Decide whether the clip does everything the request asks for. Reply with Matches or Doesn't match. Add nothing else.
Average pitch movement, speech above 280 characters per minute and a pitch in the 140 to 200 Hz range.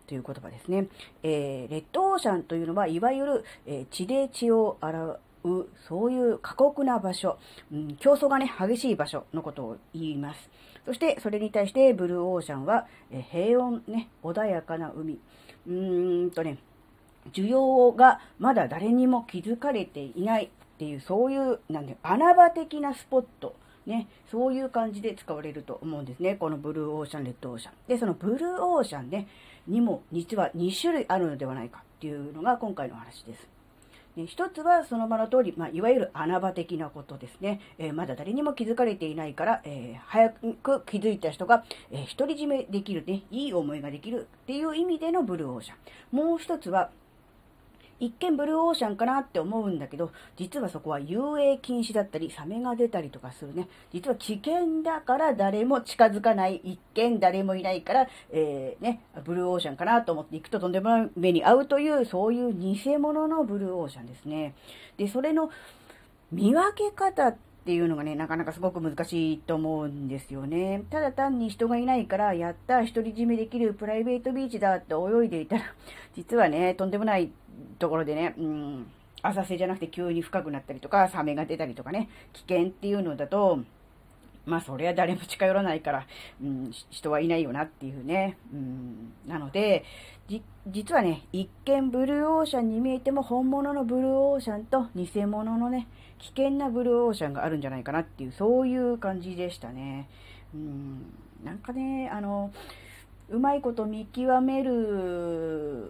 Doesn't match